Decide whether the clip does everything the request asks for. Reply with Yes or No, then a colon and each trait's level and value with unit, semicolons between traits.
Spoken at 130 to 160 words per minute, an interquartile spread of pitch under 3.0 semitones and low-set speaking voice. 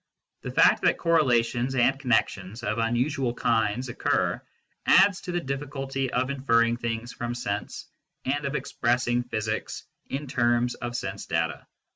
Yes: average, 145 wpm; narrow, 2.6 semitones; low, 120 Hz